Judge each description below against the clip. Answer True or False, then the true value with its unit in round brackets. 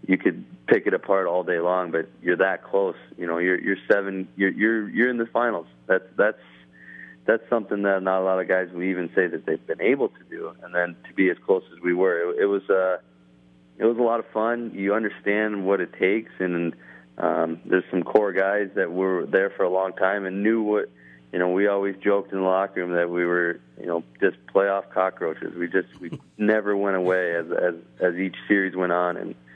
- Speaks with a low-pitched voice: True (95 Hz)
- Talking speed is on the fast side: True (230 wpm)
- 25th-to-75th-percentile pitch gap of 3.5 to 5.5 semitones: False (2.7 semitones)